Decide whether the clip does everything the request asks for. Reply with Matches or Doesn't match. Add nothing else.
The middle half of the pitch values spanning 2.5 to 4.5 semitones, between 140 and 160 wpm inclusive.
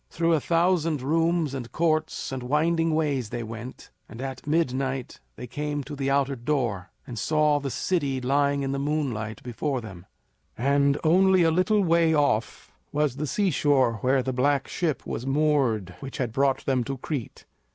Doesn't match